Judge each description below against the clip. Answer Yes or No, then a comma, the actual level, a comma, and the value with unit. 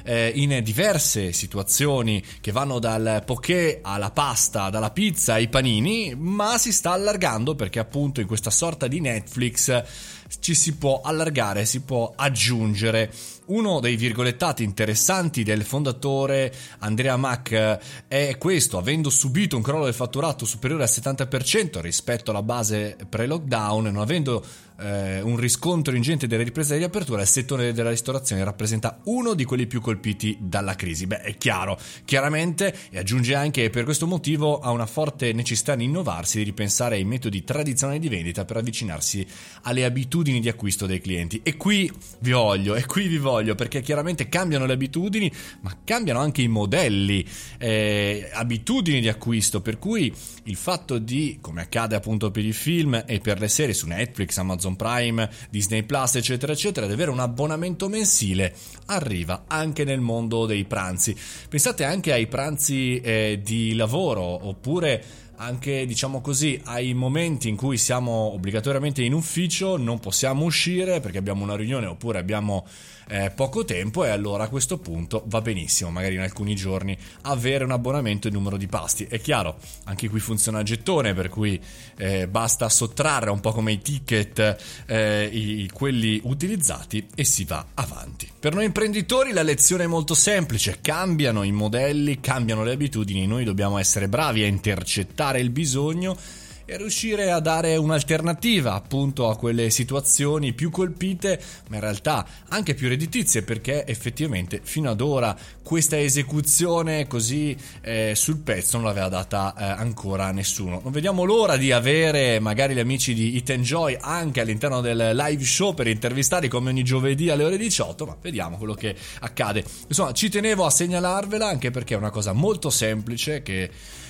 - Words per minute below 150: No, average, 160 wpm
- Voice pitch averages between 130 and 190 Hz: No, low, 120 Hz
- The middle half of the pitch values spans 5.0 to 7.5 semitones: Yes, wide, 5.6 semitones